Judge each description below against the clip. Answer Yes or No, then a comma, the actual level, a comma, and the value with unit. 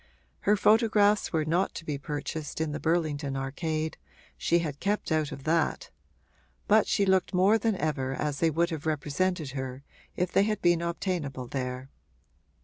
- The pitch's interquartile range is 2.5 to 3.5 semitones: No, average, 4.4 semitones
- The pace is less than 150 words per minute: No, average, 165 wpm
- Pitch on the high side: No, medium, 160 Hz